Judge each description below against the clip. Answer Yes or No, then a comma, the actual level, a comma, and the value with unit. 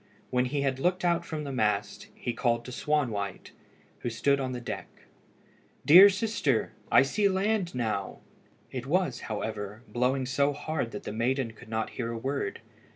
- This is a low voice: Yes, low, 130 Hz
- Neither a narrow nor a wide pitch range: Yes, average, 4.5 semitones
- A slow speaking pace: No, average, 170 wpm